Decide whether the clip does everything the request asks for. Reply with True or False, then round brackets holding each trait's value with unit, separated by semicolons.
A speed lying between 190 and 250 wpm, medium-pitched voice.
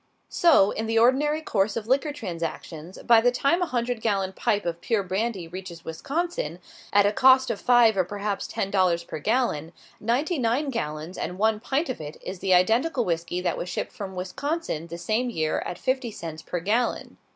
False (195 wpm; 210 Hz)